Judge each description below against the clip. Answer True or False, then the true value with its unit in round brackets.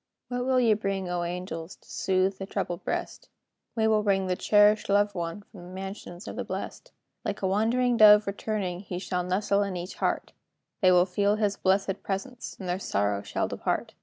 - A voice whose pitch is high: True (195 Hz)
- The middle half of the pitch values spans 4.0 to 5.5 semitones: False (2.5 semitones)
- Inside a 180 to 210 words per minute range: True (195 wpm)